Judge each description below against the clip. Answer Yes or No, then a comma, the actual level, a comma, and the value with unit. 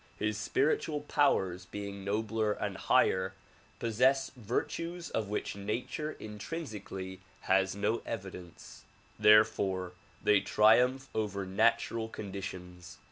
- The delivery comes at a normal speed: No, slow, 100 wpm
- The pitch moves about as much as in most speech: Yes, average, 3.4 semitones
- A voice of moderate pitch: No, low, 105 Hz